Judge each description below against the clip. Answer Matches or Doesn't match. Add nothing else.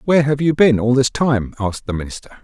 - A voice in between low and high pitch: Doesn't match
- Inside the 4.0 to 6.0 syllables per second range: Doesn't match